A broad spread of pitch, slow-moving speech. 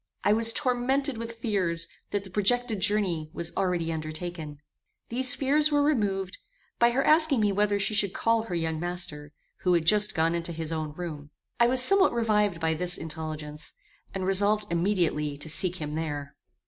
No: wide, 5.8 semitones; average, 175 wpm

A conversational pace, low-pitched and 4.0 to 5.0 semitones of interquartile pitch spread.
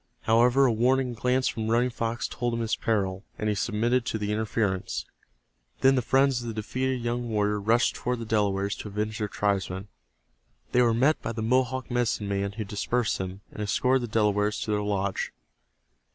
No: average, 190 wpm; low, 110 Hz; average, 2.8 semitones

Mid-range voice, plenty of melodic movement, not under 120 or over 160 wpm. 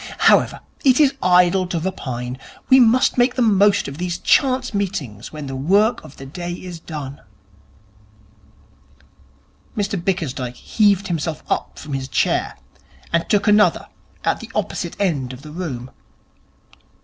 Yes: medium, 175 Hz; wide, 6.5 semitones; average, 145 wpm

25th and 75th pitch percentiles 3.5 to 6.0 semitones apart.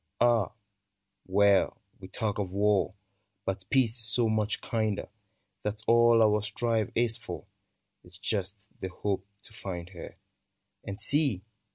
No: average, 2.9 semitones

